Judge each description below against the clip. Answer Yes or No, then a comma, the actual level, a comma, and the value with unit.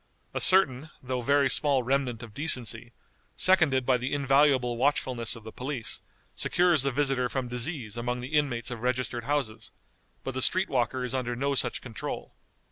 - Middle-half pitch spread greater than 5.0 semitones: No, narrow, 2.6 semitones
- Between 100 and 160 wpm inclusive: No, average, 170 wpm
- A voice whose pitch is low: Yes, low, 130 Hz